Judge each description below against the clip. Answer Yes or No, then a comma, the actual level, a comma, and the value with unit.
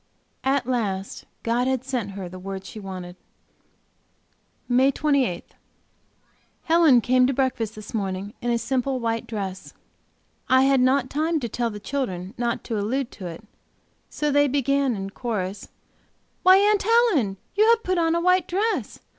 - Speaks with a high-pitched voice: Yes, very high, 250 Hz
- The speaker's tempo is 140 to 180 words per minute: Yes, average, 160 wpm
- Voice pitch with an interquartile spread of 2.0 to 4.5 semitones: No, wide, 5.5 semitones